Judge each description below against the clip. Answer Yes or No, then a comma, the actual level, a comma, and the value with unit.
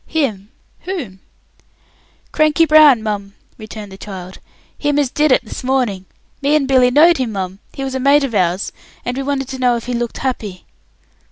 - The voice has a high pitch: Yes, very high, 250 Hz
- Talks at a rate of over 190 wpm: No, average, 185 wpm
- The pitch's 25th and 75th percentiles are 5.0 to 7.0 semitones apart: Yes, average, 5.3 semitones